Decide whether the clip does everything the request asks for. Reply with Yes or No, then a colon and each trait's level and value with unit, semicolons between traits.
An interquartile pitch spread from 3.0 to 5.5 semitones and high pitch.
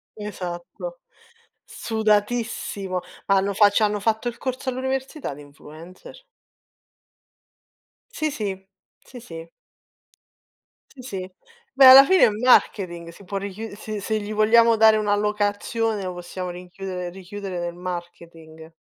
Yes: average, 3.7 semitones; high, 205 Hz